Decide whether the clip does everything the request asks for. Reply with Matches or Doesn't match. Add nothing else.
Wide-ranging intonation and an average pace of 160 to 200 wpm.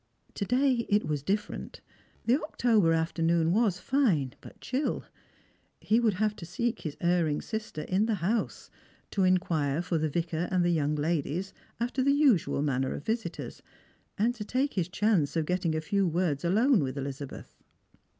Matches